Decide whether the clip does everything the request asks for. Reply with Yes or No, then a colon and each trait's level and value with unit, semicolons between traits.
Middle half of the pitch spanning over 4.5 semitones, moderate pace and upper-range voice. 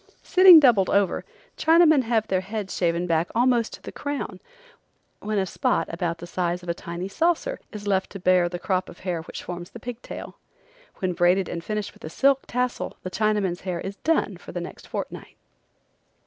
Yes: average, 5.2 semitones; average, 195 wpm; high, 195 Hz